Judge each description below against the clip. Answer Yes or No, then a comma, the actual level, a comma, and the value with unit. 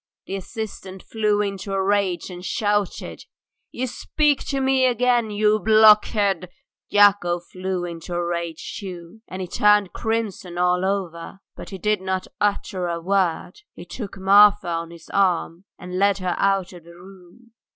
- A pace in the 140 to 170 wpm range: Yes, average, 160 wpm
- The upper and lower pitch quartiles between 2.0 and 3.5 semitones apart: Yes, average, 2.8 semitones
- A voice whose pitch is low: No, high, 195 Hz